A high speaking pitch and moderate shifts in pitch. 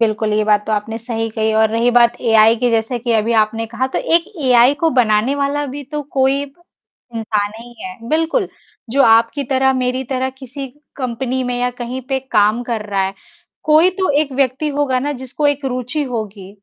Yes: high, 245 Hz; average, 3.2 semitones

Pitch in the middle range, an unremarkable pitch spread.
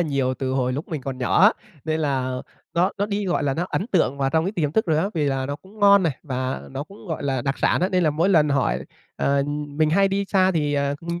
Yes: medium, 150 Hz; average, 4.9 semitones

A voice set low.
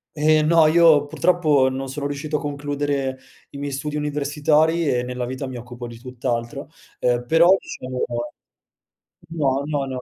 No: medium, 145 Hz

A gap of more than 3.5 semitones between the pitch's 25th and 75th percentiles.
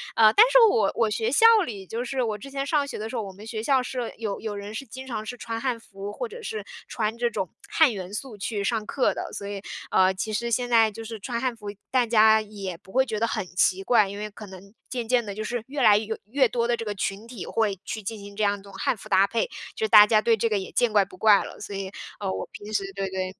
No: average, 2.9 semitones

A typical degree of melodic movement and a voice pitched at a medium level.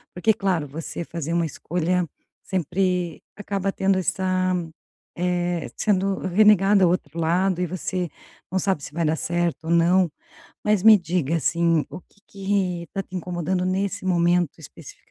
No: narrow, 2.1 semitones; medium, 180 Hz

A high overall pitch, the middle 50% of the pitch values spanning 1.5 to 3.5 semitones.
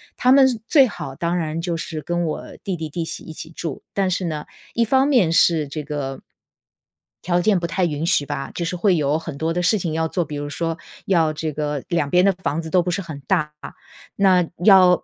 No: medium, 170 Hz; average, 3.0 semitones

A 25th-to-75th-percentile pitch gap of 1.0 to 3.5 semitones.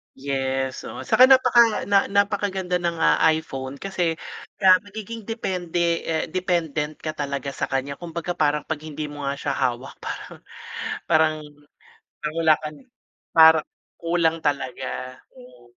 No: average, 4.7 semitones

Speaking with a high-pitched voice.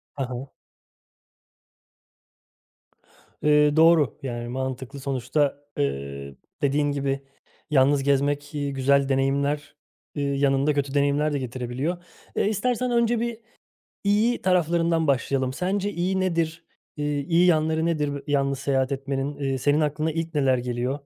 No: medium, 145 Hz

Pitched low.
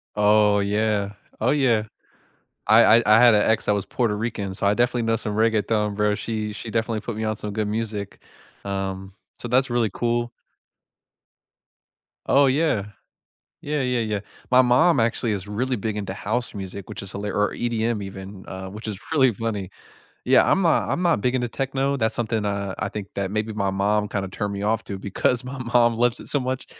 Yes: low, 110 Hz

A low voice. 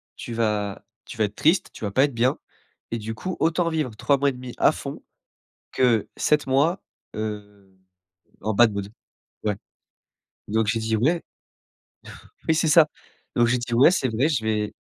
Yes: low, 120 Hz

